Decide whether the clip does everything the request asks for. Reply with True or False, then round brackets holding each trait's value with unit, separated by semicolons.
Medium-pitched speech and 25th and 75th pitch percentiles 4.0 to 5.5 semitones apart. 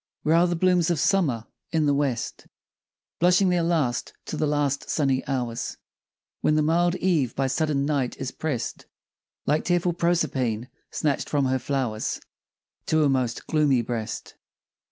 True (145 Hz; 4.4 semitones)